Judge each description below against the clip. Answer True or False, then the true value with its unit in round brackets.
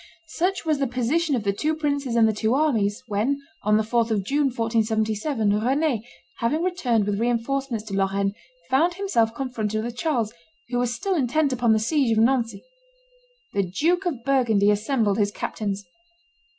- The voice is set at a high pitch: True (235 Hz)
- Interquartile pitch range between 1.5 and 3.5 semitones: False (4.5 semitones)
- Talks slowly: False (175 wpm)